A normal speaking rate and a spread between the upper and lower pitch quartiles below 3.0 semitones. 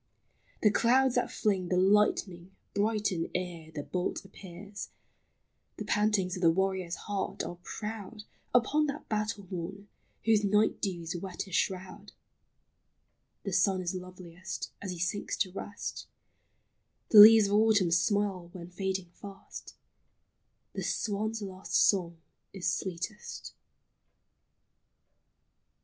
No: slow, 120 wpm; narrow, 2.6 semitones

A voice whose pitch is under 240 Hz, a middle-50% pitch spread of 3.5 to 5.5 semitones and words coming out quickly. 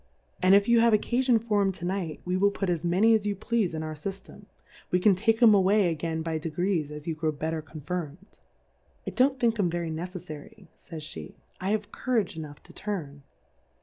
Yes: medium, 185 Hz; average, 4.5 semitones; fast, 215 wpm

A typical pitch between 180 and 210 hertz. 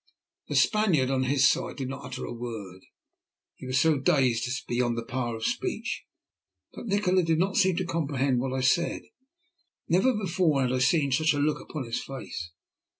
No: low, 135 Hz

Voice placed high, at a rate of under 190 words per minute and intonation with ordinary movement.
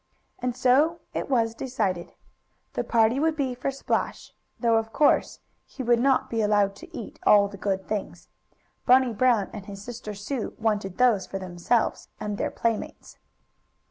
Yes: high, 225 Hz; average, 165 wpm; average, 3.7 semitones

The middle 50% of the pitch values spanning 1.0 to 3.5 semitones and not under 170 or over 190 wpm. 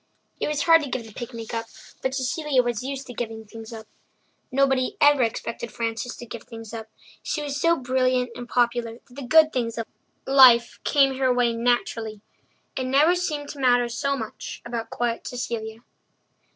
Yes: average, 2.8 semitones; average, 180 wpm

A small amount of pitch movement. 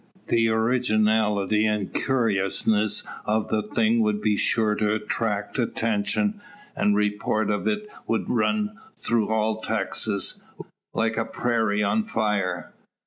Yes: narrow, 1.4 semitones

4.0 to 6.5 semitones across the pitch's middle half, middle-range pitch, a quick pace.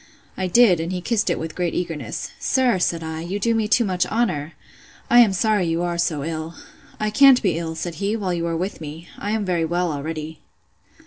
Yes: average, 4.3 semitones; medium, 175 Hz; fast, 210 wpm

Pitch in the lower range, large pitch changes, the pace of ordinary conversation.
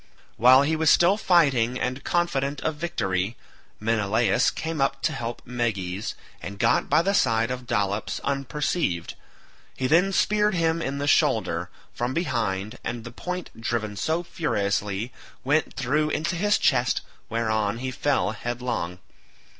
Yes: low, 125 Hz; wide, 6.1 semitones; average, 145 wpm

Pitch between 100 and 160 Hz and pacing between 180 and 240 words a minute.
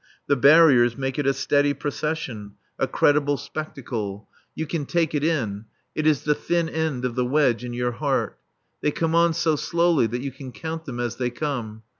Yes: medium, 140 Hz; average, 195 wpm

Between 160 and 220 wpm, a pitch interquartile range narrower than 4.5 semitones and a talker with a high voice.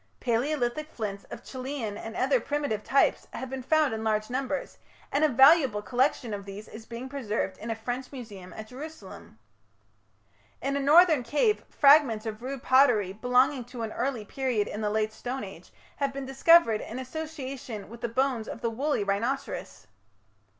Yes: average, 170 wpm; average, 4.0 semitones; very high, 250 Hz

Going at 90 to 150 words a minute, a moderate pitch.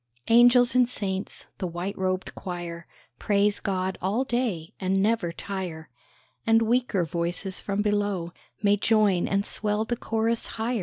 No: average, 145 wpm; high, 200 Hz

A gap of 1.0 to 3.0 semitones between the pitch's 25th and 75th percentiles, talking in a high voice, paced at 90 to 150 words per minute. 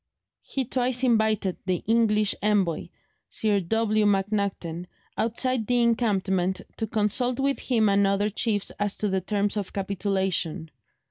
Yes: average, 2.7 semitones; high, 210 Hz; slow, 135 wpm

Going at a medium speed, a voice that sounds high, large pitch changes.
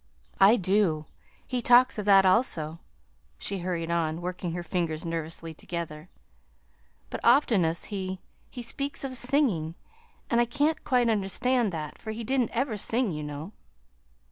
Yes: average, 145 wpm; high, 195 Hz; wide, 6.4 semitones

